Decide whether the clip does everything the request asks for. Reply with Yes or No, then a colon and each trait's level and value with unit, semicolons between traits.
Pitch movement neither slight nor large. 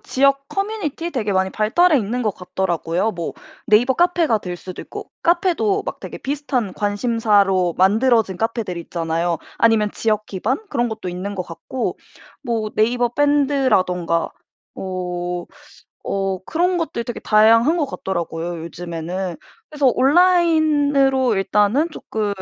No: wide, 6.9 semitones